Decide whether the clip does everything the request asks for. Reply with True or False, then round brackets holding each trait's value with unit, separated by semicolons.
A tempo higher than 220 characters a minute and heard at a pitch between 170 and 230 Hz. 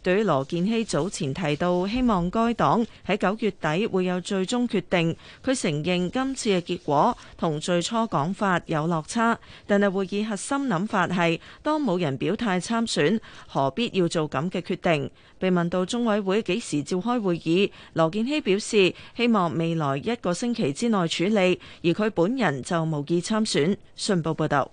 True (255 characters per minute; 185 Hz)